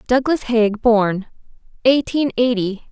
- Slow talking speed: Yes, slow, 105 wpm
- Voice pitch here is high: Yes, high, 235 Hz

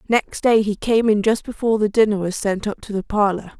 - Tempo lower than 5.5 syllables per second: No, 5.6 syllables/s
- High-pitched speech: Yes, high, 210 Hz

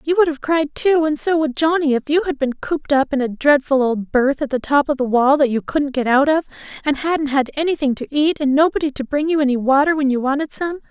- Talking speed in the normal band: No, fast, 270 wpm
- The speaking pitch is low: No, very high, 285 Hz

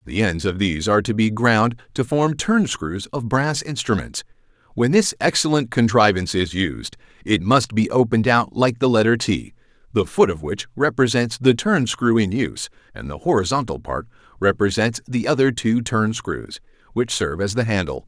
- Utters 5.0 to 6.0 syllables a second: Yes, 5.1 syllables/s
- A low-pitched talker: Yes, low, 115 Hz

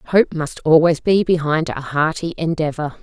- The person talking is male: No, female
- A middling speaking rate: Yes, average, 160 wpm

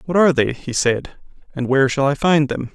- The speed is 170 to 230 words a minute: No, fast, 240 wpm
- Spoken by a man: Yes, male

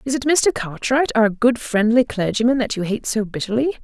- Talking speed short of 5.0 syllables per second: No, 5.4 syllables/s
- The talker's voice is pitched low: No, high, 235 Hz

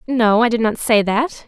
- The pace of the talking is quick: Yes, fast, 245 wpm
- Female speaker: Yes, female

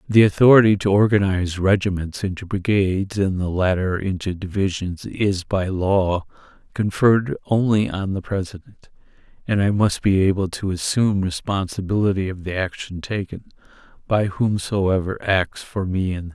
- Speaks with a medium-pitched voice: No, very low, 95 Hz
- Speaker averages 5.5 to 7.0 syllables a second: No, 5.0 syllables/s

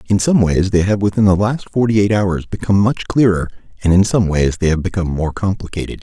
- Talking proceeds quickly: Yes, fast, 230 wpm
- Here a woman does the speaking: No, male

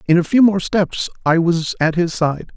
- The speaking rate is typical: No, fast, 235 wpm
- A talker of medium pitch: Yes, medium, 175 Hz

